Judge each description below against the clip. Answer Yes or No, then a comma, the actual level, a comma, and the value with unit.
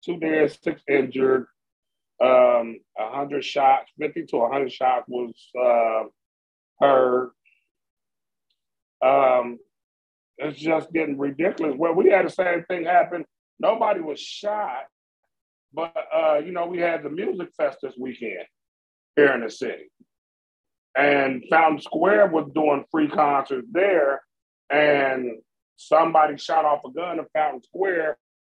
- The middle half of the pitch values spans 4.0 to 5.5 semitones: Yes, average, 4.7 semitones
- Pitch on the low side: No, medium, 145 Hz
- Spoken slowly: Yes, slow, 130 wpm